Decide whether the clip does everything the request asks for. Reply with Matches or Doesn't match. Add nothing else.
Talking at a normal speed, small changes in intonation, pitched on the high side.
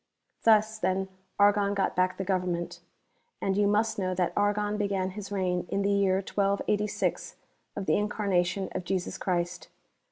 Matches